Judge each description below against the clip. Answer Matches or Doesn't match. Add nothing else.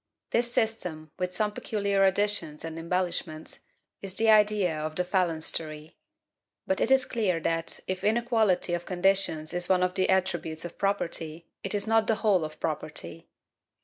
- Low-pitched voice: Doesn't match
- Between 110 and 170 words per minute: Matches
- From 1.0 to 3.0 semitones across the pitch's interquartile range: Doesn't match